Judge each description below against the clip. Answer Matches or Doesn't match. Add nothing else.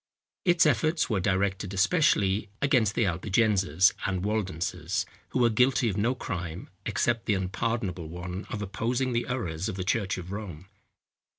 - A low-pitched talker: Matches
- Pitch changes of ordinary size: Matches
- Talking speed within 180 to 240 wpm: Doesn't match